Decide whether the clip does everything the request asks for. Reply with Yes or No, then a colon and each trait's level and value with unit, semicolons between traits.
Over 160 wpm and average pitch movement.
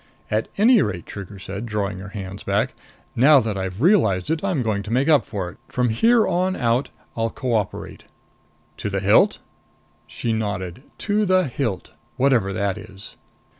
No: average, 170 wpm; wide, 6.3 semitones